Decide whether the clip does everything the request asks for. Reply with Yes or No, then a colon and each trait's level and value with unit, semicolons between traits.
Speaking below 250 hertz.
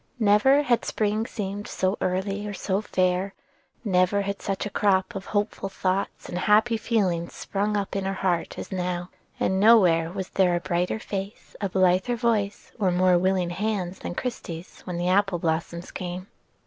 Yes: high, 190 Hz